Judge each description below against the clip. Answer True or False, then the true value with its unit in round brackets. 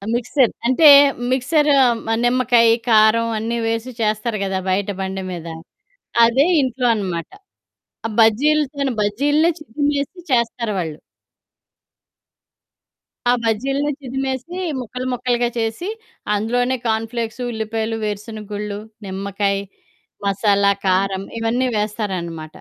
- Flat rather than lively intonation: False (3.7 semitones)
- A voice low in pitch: False (225 Hz)